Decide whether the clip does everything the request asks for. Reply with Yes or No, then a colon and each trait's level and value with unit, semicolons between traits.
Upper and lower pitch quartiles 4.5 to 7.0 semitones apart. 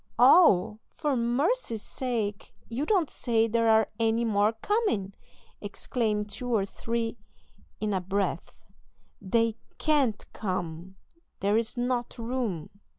No: average, 3.2 semitones